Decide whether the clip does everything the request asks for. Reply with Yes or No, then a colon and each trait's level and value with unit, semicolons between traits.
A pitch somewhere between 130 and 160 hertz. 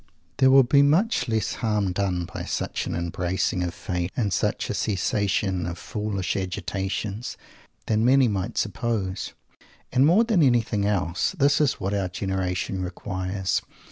No: low, 100 Hz